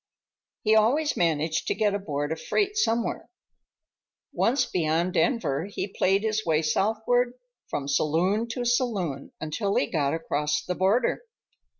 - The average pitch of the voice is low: No, high, 195 Hz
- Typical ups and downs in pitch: No, wide, 6.5 semitones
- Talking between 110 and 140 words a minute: Yes, slow, 135 wpm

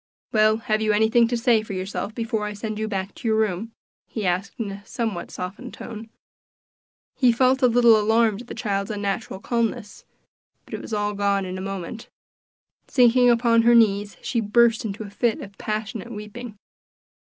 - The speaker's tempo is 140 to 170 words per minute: No, average, 185 wpm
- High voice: Yes, high, 220 Hz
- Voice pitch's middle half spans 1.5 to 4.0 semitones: Yes, narrow, 2.5 semitones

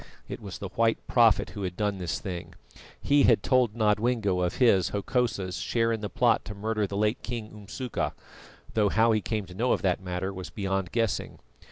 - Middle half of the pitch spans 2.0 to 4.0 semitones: Yes, average, 3.1 semitones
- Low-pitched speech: Yes, low, 105 Hz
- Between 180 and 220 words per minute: Yes, average, 200 wpm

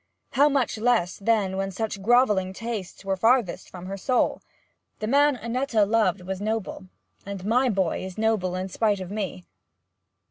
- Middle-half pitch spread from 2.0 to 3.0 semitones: No, average, 3.5 semitones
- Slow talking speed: No, average, 165 wpm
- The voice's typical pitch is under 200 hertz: No, high, 210 Hz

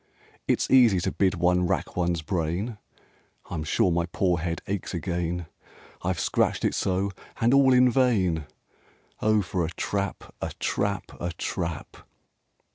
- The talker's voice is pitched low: Yes, very low, 90 Hz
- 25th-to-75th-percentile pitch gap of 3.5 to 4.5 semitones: No, average, 3.0 semitones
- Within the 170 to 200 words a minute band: No, average, 145 wpm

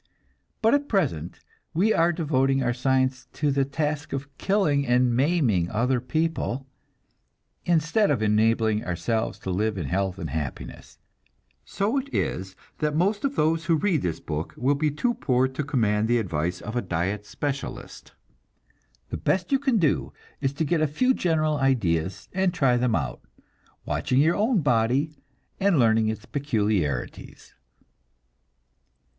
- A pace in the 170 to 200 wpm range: No, average, 150 wpm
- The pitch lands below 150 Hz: Yes, low, 135 Hz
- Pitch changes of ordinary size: No, wide, 6.8 semitones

